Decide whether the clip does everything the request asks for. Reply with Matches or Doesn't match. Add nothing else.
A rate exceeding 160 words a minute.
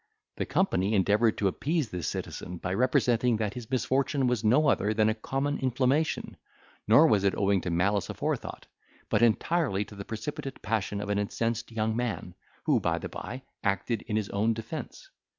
Matches